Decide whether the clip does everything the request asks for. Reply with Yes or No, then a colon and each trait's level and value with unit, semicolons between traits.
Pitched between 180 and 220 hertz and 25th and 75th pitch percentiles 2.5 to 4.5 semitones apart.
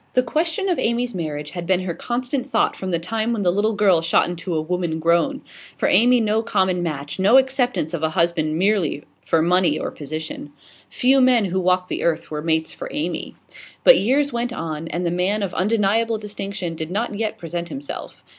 No: medium, 185 Hz; wide, 5.6 semitones